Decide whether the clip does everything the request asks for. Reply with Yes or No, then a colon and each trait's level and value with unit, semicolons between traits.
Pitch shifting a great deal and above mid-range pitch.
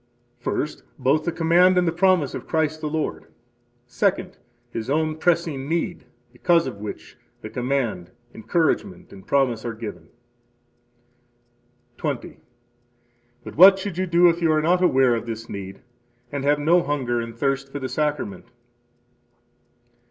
No: wide, 5.7 semitones; medium, 145 Hz